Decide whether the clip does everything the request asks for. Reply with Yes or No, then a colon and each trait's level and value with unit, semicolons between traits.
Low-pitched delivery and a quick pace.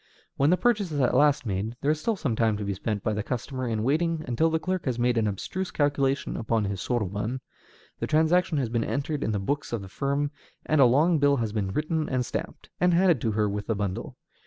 Yes: low, 130 Hz; fast, 240 wpm